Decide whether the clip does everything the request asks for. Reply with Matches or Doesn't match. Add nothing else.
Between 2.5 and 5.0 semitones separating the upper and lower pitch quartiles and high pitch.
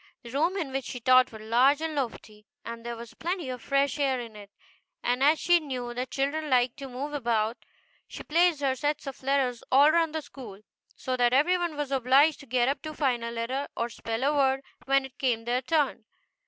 Matches